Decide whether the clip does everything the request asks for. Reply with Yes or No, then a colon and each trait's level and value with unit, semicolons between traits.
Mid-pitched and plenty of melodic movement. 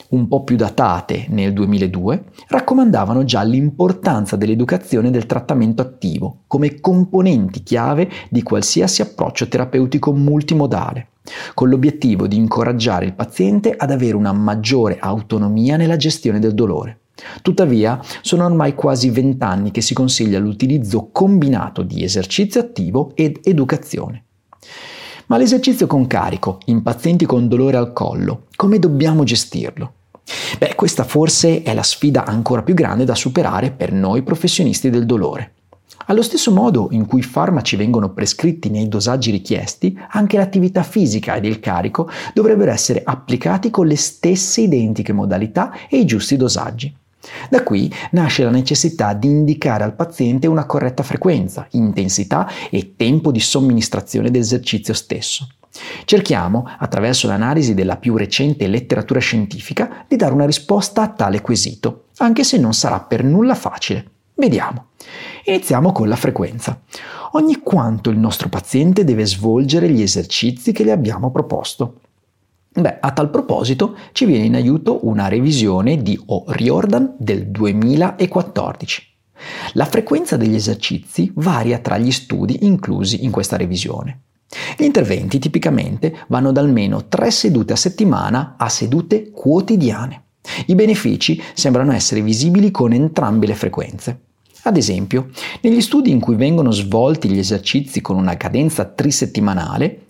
No: low, 130 Hz; wide, 7.1 semitones